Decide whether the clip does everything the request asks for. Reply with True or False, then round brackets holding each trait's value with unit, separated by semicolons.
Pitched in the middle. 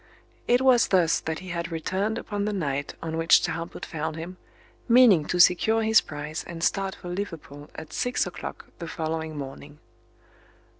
True (170 Hz)